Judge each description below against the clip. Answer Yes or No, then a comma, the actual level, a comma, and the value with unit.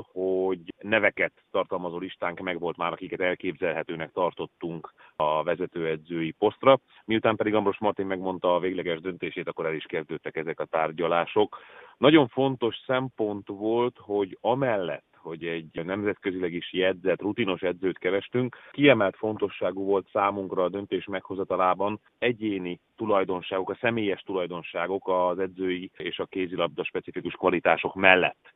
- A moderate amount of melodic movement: Yes, average, 3.2 semitones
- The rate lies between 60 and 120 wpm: No, average, 130 wpm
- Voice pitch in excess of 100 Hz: No, very low, 95 Hz